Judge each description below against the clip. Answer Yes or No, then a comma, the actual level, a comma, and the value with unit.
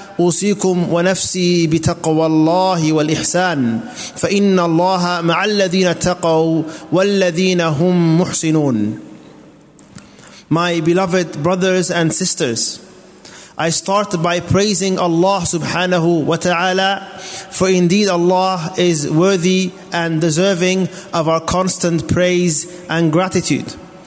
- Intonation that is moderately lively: No, narrow, 2.0 semitones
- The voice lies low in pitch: No, medium, 175 Hz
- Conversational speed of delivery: No, slow, 95 wpm